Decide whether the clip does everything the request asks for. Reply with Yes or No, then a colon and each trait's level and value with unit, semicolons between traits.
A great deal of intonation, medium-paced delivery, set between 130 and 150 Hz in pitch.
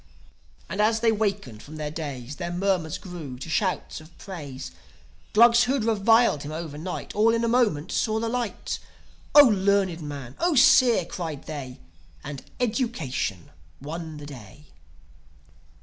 No: wide, 7.2 semitones; average, 145 wpm; medium, 175 Hz